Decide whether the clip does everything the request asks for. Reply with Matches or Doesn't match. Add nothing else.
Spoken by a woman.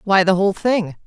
Matches